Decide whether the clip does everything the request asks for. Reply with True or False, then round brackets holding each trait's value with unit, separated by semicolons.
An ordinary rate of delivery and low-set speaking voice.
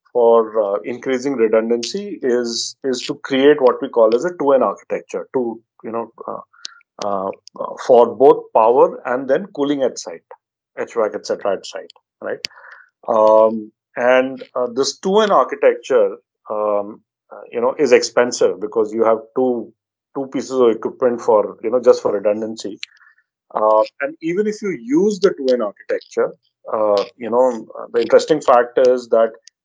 False (160 wpm; 190 Hz)